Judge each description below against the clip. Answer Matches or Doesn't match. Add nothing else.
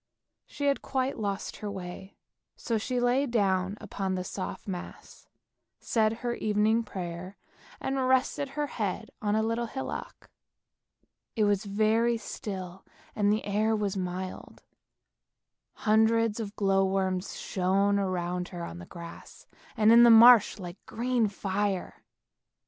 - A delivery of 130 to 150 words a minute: Matches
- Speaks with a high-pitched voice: Matches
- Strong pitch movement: Doesn't match